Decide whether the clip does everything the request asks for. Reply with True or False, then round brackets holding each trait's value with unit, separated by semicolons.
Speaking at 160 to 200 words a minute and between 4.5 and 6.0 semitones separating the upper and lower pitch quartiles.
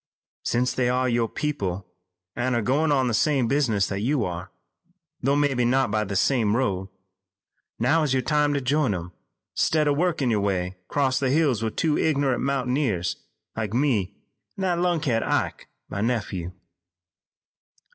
True (165 wpm; 5.2 semitones)